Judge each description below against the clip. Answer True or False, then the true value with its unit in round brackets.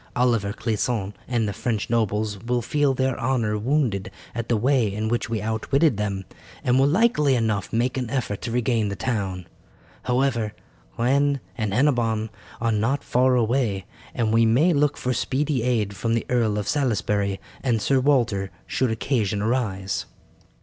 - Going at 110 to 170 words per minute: True (165 wpm)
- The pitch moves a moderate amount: True (3.6 semitones)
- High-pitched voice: False (115 Hz)